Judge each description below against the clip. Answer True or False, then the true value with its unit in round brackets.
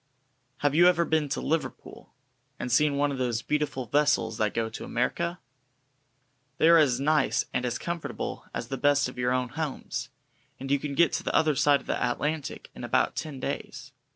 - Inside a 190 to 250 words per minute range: True (195 wpm)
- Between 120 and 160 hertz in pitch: True (140 Hz)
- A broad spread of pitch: False (3.5 semitones)